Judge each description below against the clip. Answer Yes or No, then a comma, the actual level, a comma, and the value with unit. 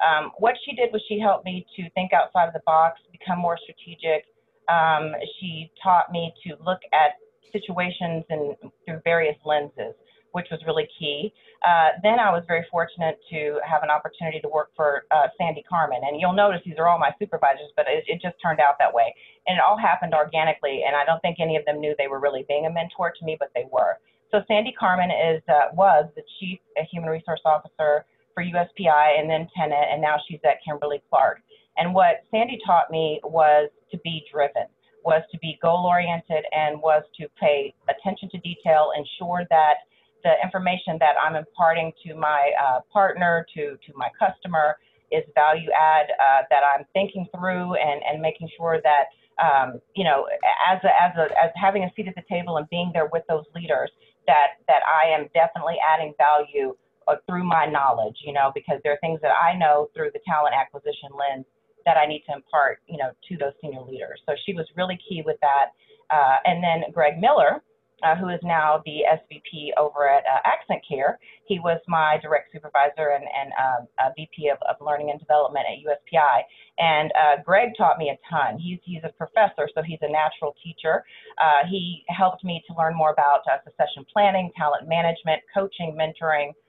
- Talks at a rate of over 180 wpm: Yes, average, 200 wpm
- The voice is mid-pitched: Yes, medium, 160 Hz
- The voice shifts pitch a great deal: No, average, 3.1 semitones